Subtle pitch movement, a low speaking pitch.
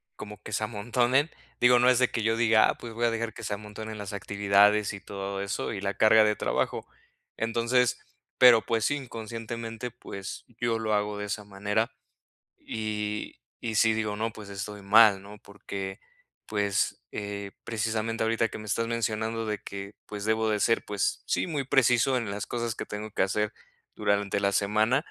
Yes: narrow, 2.1 semitones; low, 110 Hz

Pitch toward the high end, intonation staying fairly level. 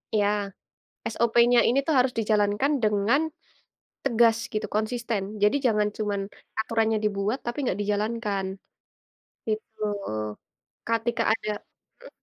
Yes: high, 220 Hz; narrow, 2.3 semitones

